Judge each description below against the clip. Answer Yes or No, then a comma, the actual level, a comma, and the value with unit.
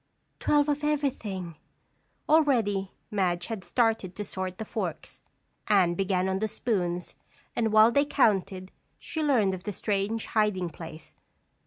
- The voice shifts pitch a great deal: No, average, 3.7 semitones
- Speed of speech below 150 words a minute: Yes, average, 140 wpm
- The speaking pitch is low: No, high, 205 Hz